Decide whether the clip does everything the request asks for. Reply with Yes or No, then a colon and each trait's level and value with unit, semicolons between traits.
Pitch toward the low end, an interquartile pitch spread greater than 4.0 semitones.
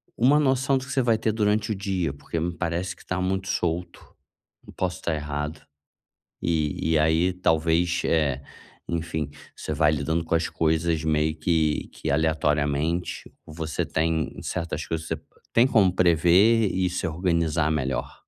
No: very low, 85 Hz; average, 2.9 semitones